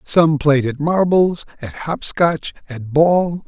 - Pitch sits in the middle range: Yes, medium, 155 Hz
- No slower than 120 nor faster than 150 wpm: Yes, average, 140 wpm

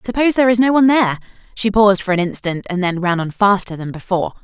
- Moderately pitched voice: No, high, 205 Hz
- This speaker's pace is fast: Yes, fast, 245 wpm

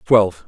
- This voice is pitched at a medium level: No, low, 110 Hz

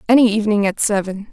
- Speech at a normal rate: Yes, average, 180 wpm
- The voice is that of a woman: Yes, female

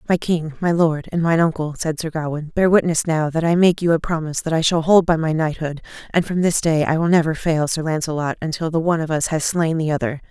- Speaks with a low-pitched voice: No, medium, 160 Hz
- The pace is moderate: No, fast, 260 wpm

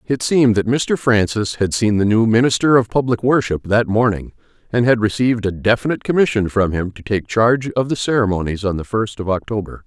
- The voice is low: Yes, low, 110 Hz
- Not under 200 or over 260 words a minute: Yes, fast, 205 wpm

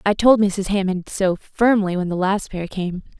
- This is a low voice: No, high, 195 Hz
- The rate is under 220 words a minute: Yes, fast, 205 wpm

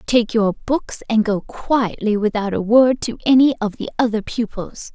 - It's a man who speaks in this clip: No, female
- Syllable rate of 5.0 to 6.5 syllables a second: No, 4.6 syllables/s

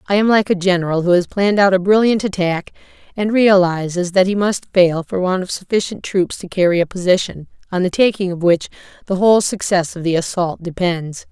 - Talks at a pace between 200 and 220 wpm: Yes, fast, 205 wpm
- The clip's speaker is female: Yes, female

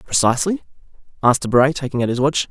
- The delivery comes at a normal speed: Yes, average, 170 wpm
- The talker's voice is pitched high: No, low, 135 Hz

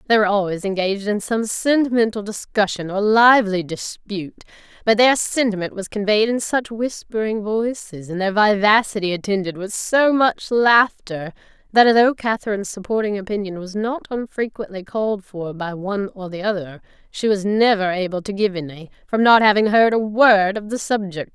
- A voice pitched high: Yes, high, 205 Hz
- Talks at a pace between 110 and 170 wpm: Yes, average, 165 wpm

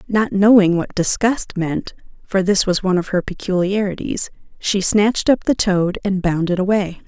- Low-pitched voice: No, high, 195 Hz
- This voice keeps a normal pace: Yes, average, 170 wpm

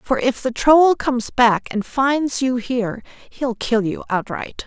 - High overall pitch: Yes, very high, 255 Hz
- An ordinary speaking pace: Yes, average, 180 wpm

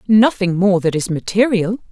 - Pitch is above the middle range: Yes, high, 195 Hz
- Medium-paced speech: Yes, average, 155 wpm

